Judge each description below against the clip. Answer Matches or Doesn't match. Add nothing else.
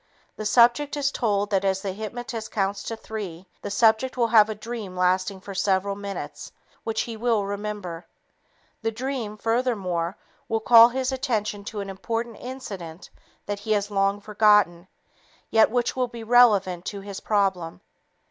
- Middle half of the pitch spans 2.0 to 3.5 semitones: Matches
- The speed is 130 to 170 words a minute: Matches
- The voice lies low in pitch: Doesn't match